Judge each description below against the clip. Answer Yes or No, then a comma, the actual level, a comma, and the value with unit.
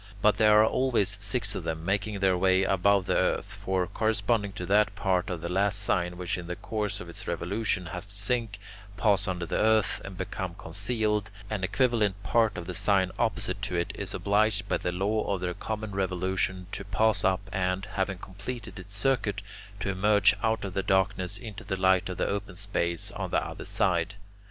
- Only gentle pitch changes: Yes, narrow, 2.3 semitones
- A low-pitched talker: Yes, low, 100 Hz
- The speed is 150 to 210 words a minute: Yes, average, 200 wpm